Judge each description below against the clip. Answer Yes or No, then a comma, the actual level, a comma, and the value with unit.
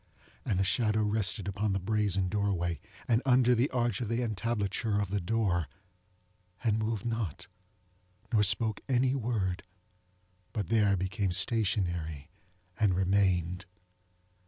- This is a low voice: Yes, low, 105 Hz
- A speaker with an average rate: No, slow, 130 wpm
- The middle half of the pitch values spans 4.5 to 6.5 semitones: No, average, 3.3 semitones